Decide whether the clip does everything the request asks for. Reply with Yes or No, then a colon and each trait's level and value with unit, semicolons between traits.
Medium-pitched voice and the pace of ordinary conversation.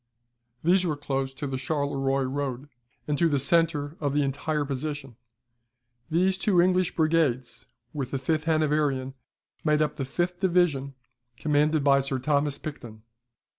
Yes: medium, 145 Hz; average, 145 wpm